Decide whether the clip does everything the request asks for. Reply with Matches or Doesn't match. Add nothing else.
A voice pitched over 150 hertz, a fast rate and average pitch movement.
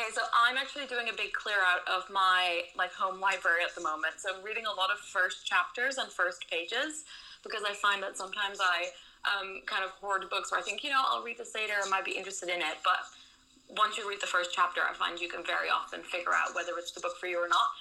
Matches